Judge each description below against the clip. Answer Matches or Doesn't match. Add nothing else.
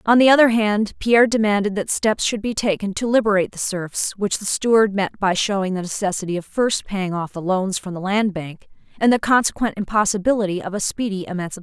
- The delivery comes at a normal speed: Doesn't match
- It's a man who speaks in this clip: Doesn't match